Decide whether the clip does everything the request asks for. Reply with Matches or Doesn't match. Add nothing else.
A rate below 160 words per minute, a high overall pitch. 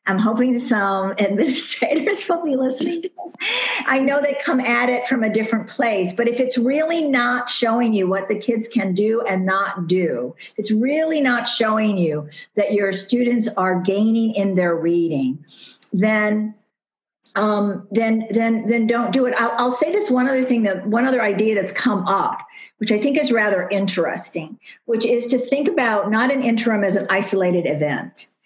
Doesn't match